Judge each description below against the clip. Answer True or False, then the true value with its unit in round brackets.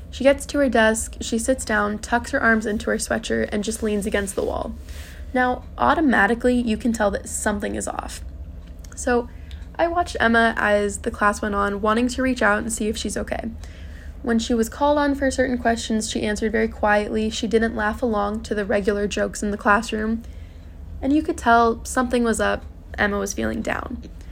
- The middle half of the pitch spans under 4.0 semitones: True (2.8 semitones)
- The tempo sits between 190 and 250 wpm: True (200 wpm)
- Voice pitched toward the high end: True (220 Hz)